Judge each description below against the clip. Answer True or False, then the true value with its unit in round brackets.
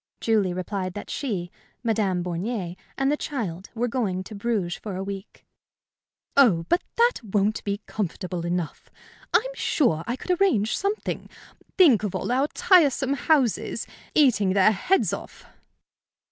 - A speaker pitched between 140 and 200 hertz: False (215 Hz)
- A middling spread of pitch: False (6.4 semitones)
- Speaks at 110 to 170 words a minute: True (145 wpm)